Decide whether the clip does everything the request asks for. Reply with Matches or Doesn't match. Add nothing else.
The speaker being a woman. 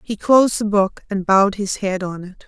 Matches